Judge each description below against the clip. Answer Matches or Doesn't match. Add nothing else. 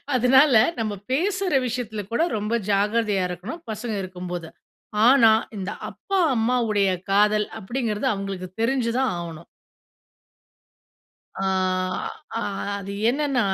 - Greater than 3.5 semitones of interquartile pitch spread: Matches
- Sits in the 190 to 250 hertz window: Matches